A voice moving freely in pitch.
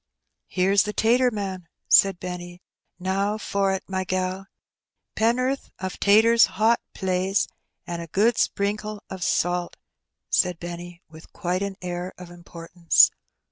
No: average, 2.7 semitones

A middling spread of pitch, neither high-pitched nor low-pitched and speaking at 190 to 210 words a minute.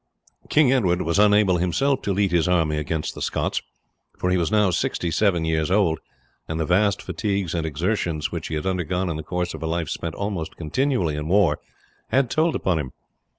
No: average, 3.9 semitones; very low, 90 Hz; average, 200 wpm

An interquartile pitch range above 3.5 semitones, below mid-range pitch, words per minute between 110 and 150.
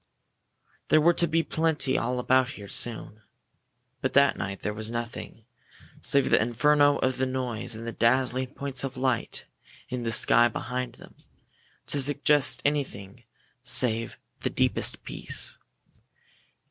No: average, 3.2 semitones; low, 125 Hz; slow, 135 wpm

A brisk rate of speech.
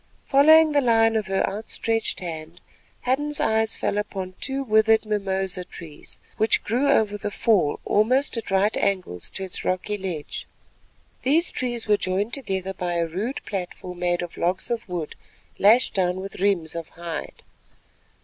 No: average, 160 wpm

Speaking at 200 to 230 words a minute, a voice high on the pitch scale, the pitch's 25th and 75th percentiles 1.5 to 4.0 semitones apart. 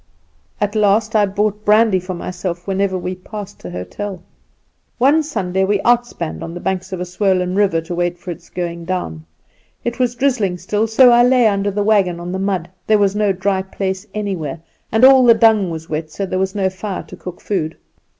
Yes: fast, 205 wpm; high, 195 Hz; average, 3.0 semitones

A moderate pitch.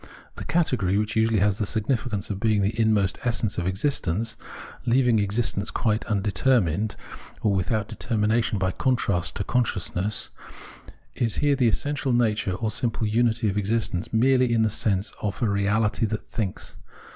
No: low, 110 Hz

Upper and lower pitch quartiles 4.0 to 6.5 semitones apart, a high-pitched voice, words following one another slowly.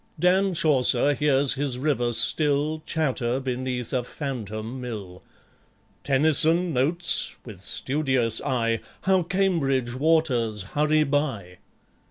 No: average, 4.3 semitones; low, 135 Hz; slow, 105 wpm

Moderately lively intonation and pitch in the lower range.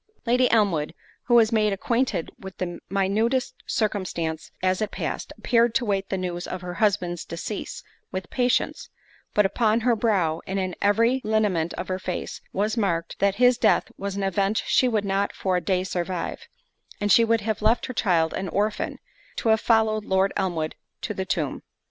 No: average, 3.2 semitones; high, 200 Hz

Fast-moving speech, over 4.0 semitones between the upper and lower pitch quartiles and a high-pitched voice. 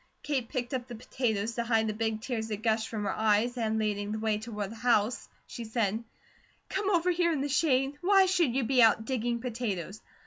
No: fast, 215 wpm; average, 3.2 semitones; high, 230 Hz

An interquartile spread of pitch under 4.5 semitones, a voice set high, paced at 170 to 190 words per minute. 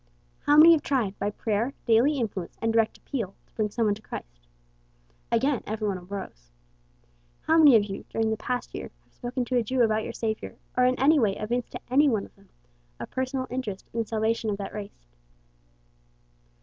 No: average, 3.6 semitones; high, 225 Hz; average, 200 wpm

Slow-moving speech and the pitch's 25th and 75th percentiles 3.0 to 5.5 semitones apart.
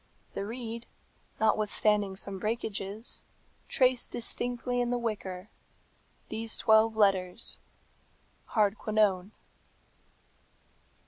No: slow, 80 wpm; narrow, 2.6 semitones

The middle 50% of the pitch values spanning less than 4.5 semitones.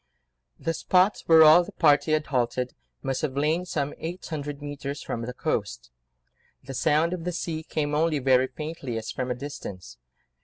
Yes: average, 3.8 semitones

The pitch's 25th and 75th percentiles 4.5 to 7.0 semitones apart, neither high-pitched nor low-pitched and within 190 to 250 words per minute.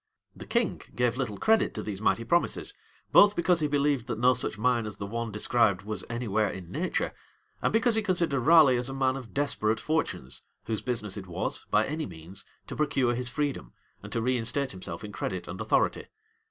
No: average, 5.0 semitones; low, 120 Hz; fast, 205 wpm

